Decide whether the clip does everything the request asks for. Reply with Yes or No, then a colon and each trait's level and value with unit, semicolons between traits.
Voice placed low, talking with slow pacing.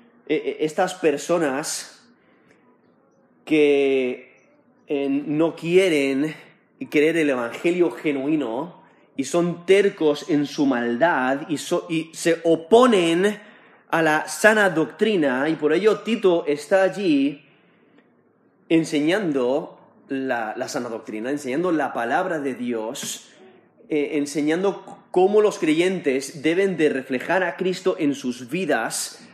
No: medium, 160 Hz; slow, 110 wpm